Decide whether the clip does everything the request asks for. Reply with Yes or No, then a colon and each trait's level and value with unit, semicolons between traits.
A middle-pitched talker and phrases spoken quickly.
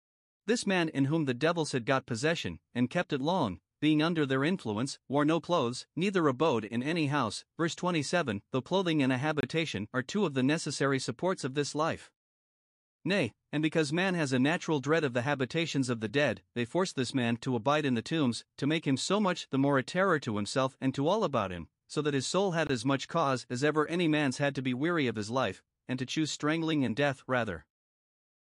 Yes: medium, 145 Hz; fast, 225 wpm